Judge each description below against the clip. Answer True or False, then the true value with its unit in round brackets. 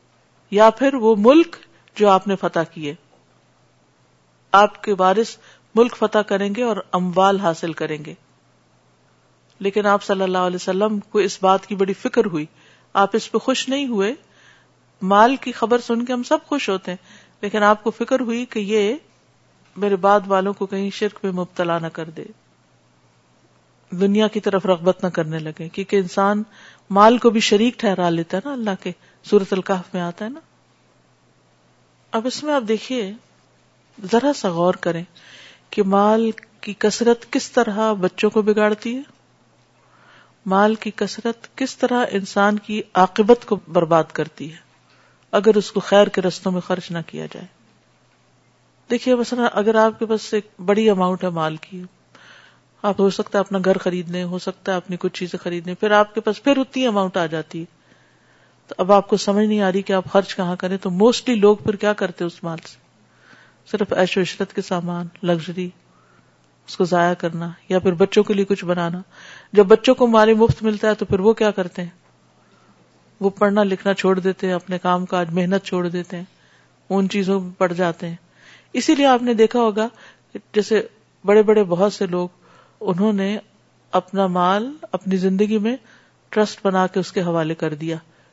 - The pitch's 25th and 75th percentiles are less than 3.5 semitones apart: True (3.1 semitones)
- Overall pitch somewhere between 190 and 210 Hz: True (195 Hz)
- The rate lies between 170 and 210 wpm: True (185 wpm)